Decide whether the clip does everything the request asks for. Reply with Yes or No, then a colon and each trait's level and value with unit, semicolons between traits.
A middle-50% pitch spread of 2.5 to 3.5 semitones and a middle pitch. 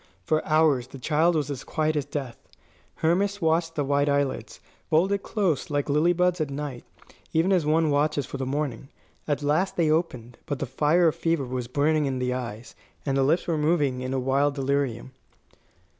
Yes: average, 3.1 semitones; medium, 145 Hz